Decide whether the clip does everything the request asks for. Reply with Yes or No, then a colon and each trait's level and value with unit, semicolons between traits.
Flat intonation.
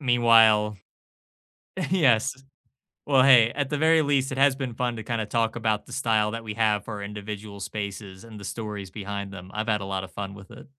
No: average, 3.1 semitones